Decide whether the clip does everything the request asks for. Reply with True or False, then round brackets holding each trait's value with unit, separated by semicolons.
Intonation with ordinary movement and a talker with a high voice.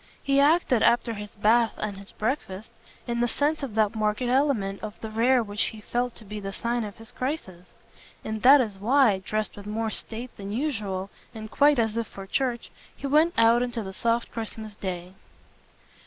True (3.2 semitones; 225 Hz)